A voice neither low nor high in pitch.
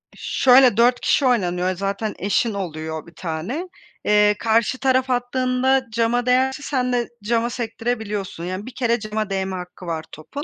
No: high, 225 Hz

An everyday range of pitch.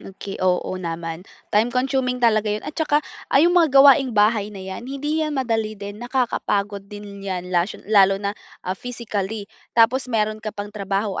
Yes: average, 4.1 semitones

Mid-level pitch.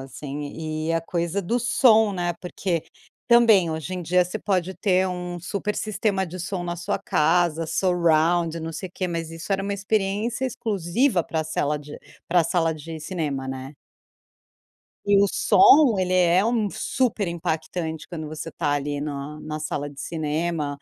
Yes: medium, 175 Hz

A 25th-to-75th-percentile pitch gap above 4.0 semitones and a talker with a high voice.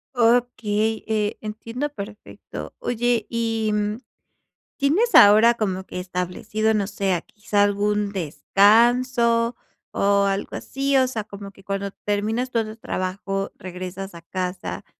No: average, 2.8 semitones; high, 210 Hz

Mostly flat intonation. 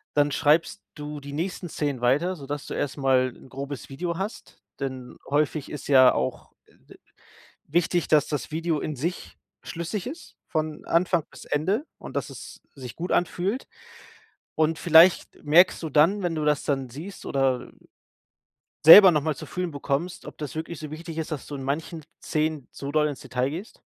No: average, 3.2 semitones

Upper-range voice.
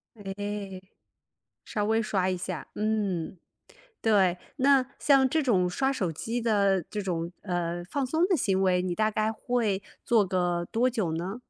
Yes: high, 205 Hz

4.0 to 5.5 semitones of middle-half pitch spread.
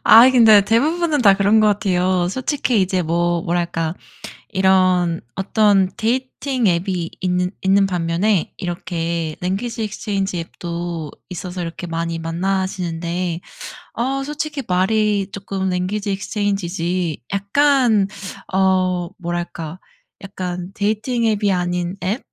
No: average, 3.3 semitones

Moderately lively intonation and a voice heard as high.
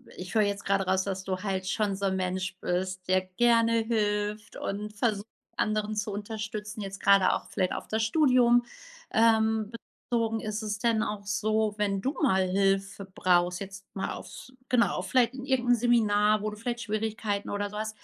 No: narrow, 2.3 semitones; high, 210 Hz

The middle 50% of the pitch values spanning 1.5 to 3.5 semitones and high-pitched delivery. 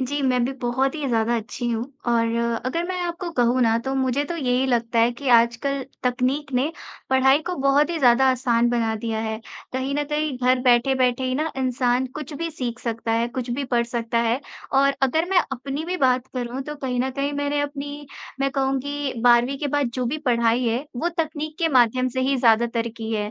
Yes: average, 3.0 semitones; very high, 260 Hz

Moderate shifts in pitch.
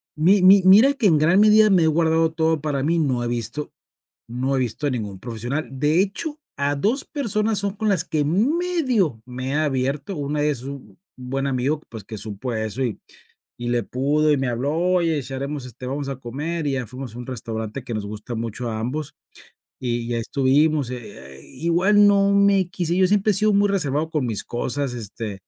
No: wide, 6.5 semitones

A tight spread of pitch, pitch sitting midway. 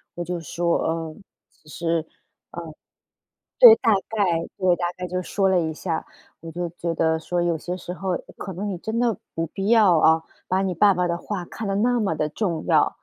No: average, 3.0 semitones; medium, 175 Hz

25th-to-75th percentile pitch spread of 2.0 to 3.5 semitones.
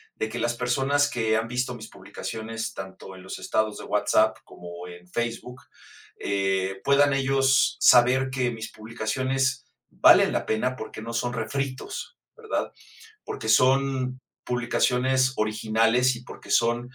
Yes: average, 2.9 semitones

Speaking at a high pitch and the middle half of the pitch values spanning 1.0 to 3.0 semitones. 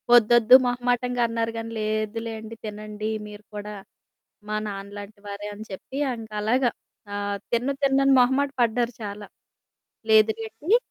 Yes: high, 220 Hz; narrow, 2.6 semitones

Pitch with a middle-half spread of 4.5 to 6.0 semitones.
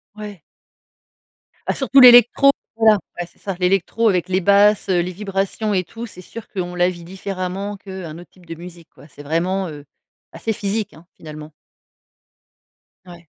No: average, 3.0 semitones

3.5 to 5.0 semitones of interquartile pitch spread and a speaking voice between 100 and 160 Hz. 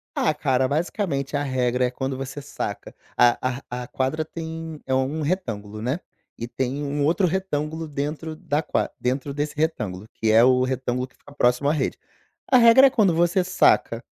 Yes: average, 4.0 semitones; medium, 140 Hz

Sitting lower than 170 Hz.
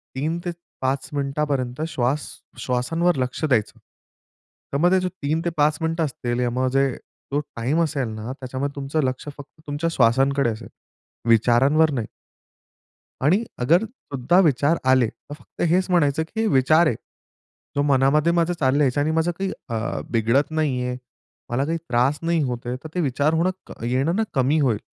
Yes: medium, 140 Hz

